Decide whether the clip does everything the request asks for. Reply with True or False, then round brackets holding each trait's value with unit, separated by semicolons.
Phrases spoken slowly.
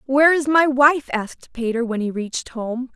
False (205 wpm)